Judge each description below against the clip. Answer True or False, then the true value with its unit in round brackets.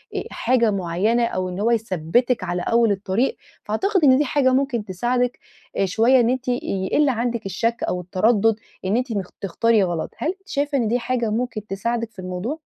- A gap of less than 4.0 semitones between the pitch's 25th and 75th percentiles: False (4.3 semitones)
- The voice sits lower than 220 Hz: False (230 Hz)